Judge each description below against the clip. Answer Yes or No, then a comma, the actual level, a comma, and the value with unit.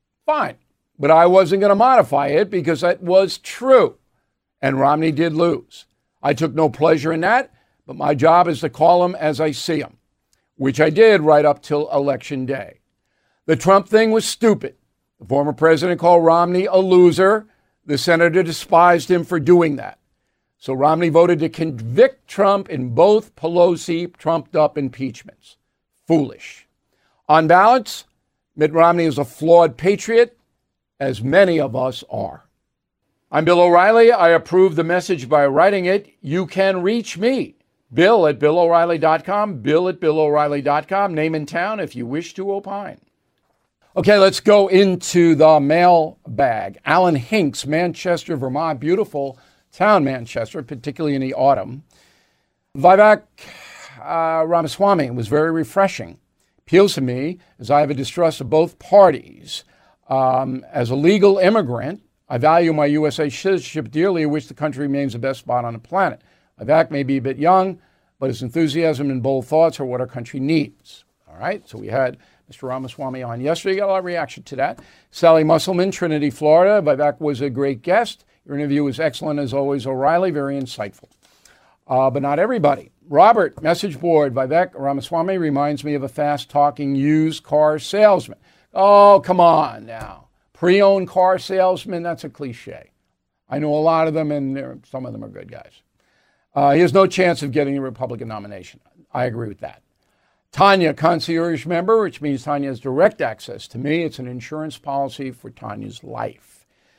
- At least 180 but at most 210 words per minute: No, average, 165 wpm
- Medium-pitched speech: Yes, medium, 160 Hz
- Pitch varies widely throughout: No, average, 4.2 semitones